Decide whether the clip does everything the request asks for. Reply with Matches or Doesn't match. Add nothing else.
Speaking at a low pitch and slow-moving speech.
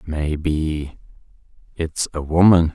Matches